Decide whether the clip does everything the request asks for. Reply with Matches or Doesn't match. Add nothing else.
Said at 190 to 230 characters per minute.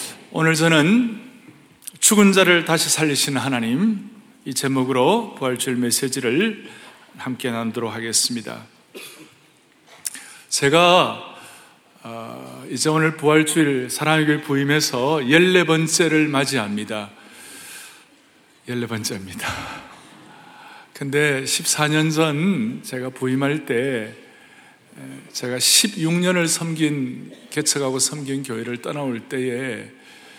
Matches